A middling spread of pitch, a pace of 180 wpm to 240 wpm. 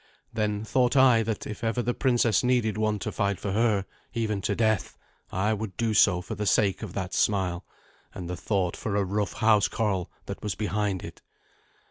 No: narrow, 2.3 semitones; average, 190 wpm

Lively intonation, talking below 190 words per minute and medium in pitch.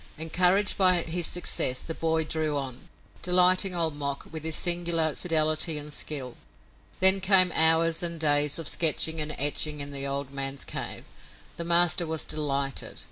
No: average, 2.9 semitones; average, 160 wpm; medium, 160 Hz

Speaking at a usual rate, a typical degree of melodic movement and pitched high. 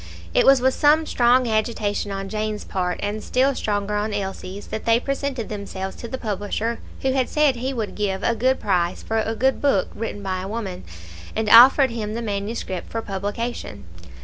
Yes: average, 190 wpm; average, 3.5 semitones; high, 220 Hz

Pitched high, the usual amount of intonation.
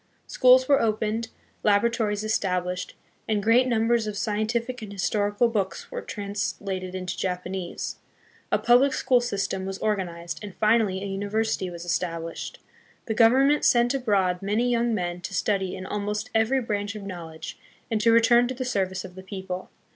Yes: high, 210 Hz; average, 3.7 semitones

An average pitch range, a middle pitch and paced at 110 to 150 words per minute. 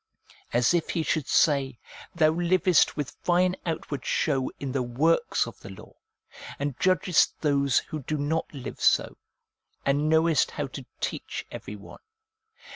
No: average, 3.3 semitones; medium, 150 Hz; average, 160 wpm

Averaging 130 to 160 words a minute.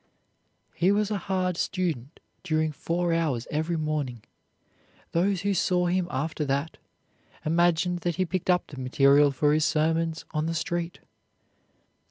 Yes: average, 150 wpm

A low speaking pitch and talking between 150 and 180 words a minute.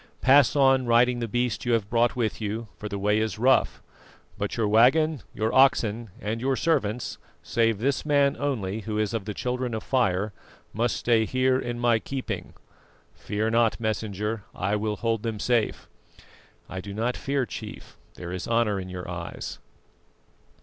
Yes: low, 115 Hz; average, 170 wpm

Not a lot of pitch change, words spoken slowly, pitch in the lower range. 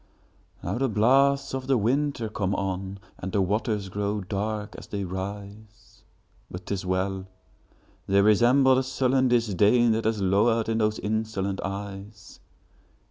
No: average, 3.2 semitones; slow, 130 wpm; low, 105 Hz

